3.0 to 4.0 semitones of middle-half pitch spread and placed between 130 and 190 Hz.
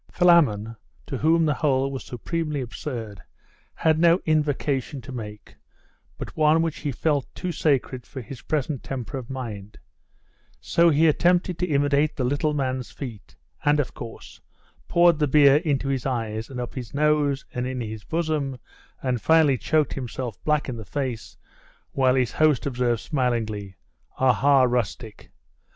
Yes: average, 3.7 semitones; low, 135 Hz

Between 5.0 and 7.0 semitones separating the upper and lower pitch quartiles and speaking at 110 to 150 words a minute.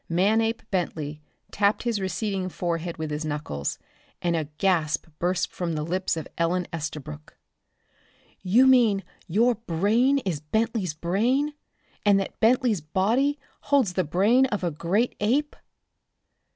Yes: wide, 5.5 semitones; slow, 135 wpm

